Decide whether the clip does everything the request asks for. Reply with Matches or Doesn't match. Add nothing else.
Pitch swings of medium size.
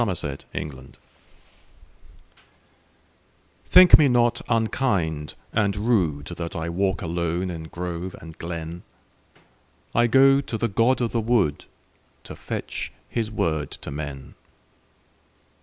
Doesn't match